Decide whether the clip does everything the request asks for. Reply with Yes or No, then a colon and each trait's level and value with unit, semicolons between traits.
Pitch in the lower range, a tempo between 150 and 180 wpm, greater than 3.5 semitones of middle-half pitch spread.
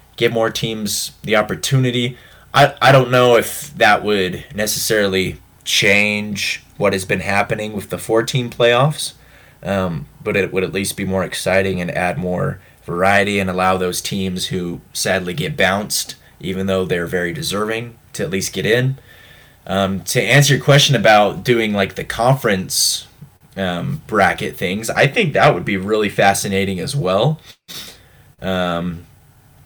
Yes: low, 100 Hz; average, 155 wpm; average, 4.2 semitones